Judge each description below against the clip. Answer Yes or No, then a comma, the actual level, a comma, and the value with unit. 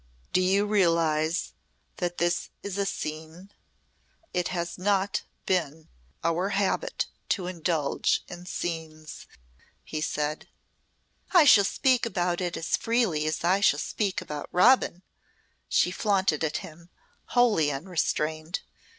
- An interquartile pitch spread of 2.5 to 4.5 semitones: Yes, average, 3.6 semitones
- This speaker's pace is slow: Yes, slow, 125 wpm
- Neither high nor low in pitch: Yes, medium, 175 Hz